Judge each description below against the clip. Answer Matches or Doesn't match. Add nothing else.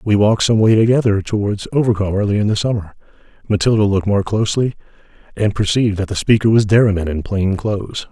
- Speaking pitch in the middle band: Doesn't match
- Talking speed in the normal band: Matches